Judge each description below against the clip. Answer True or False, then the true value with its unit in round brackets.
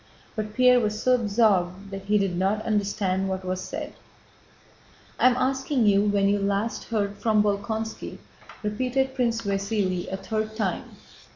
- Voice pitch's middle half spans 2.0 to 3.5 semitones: True (2.5 semitones)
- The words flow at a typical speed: True (155 wpm)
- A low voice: False (210 Hz)